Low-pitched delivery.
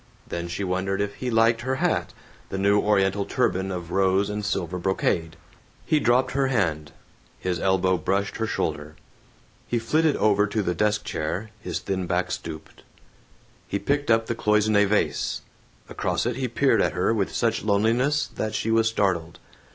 Yes: low, 100 Hz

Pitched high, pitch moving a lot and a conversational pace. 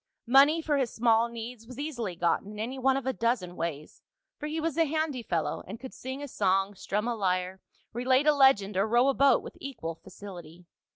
No: high, 235 Hz; wide, 5.8 semitones; fast, 215 wpm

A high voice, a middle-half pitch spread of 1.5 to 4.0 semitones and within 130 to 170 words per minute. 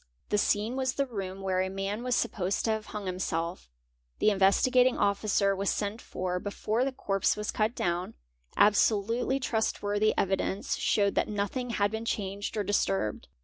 No: high, 205 Hz; narrow, 2.4 semitones; average, 180 wpm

